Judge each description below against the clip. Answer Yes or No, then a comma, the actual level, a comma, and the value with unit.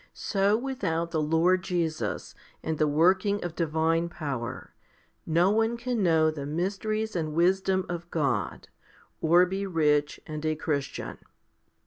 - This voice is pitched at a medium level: Yes, medium, 170 Hz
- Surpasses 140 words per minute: No, slow, 135 wpm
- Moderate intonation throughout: Yes, average, 3.5 semitones